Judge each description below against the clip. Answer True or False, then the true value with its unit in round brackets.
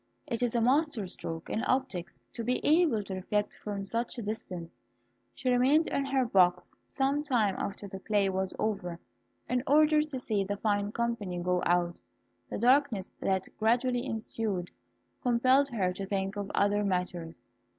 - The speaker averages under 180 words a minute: True (165 wpm)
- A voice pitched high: True (210 Hz)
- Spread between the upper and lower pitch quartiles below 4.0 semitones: False (4.8 semitones)